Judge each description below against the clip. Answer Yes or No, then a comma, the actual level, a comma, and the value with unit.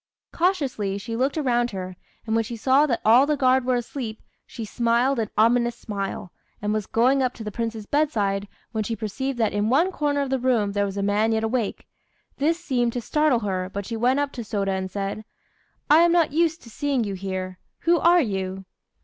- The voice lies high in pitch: Yes, high, 235 Hz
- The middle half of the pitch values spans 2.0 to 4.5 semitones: No, average, 4.9 semitones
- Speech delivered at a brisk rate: Yes, fast, 215 wpm